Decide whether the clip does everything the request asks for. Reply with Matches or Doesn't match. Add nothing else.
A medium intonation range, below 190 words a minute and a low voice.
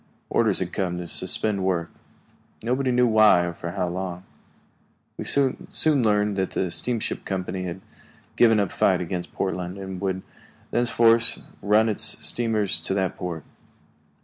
Matches